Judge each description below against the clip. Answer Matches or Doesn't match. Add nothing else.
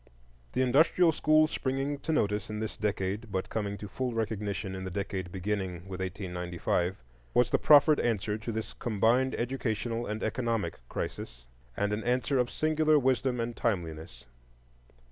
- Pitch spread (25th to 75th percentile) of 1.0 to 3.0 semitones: Doesn't match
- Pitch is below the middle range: Matches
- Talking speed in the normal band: Matches